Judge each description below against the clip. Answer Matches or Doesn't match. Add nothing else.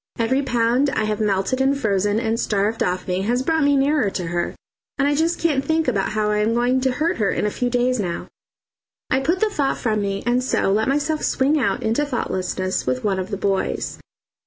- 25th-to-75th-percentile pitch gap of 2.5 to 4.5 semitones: Doesn't match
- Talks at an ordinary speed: Doesn't match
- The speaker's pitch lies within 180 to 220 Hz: Doesn't match